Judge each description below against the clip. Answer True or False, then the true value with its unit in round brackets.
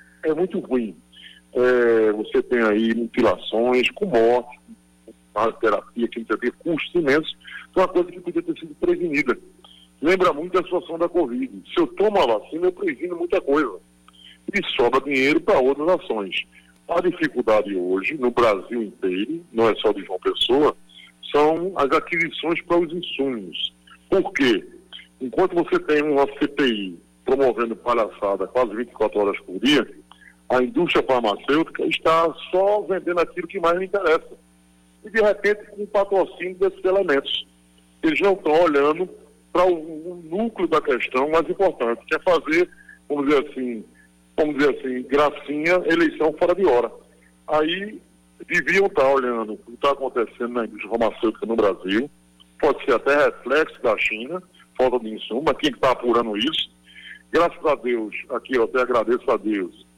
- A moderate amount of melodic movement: False (8.9 semitones)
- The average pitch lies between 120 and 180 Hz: True (140 Hz)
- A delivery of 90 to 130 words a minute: False (160 wpm)